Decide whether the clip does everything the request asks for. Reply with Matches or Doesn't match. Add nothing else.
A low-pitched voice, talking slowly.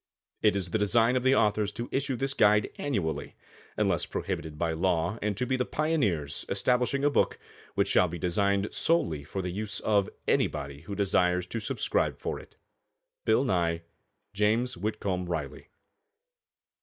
Doesn't match